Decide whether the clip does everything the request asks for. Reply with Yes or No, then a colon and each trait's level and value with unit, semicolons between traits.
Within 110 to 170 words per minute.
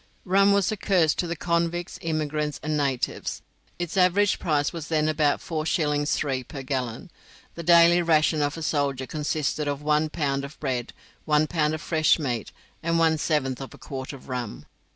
No: average, 180 wpm